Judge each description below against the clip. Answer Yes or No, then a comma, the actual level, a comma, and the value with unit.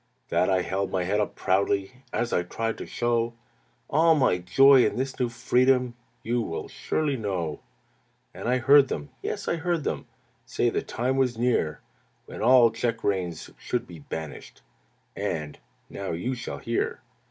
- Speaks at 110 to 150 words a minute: No, average, 165 wpm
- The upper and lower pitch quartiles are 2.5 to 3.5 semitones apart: No, wide, 5.4 semitones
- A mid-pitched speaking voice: No, low, 115 Hz